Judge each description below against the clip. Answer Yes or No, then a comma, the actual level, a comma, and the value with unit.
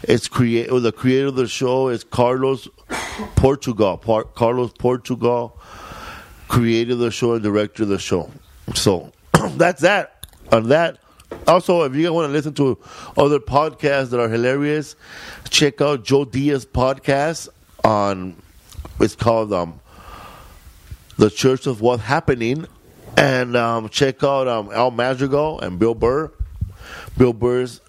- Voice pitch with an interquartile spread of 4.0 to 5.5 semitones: No, average, 3.5 semitones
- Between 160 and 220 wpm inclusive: No, average, 140 wpm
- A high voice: No, low, 125 Hz